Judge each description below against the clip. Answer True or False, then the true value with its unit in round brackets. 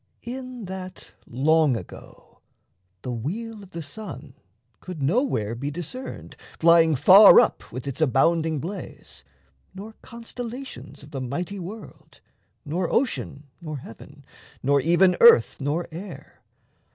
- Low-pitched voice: False (165 Hz)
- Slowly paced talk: True (125 wpm)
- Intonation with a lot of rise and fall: True (6.2 semitones)